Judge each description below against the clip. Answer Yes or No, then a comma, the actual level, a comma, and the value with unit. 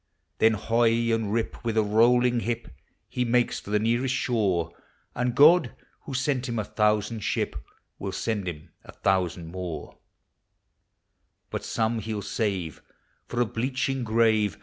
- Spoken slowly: No, average, 150 wpm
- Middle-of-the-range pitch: No, low, 115 Hz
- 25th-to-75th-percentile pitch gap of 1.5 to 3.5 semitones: Yes, average, 2.9 semitones